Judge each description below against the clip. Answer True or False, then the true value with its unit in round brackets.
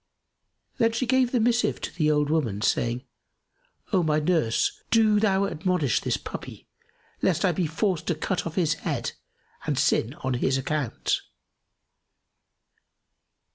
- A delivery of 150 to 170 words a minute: False (140 wpm)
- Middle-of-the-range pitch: True (160 Hz)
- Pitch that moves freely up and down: True (6.1 semitones)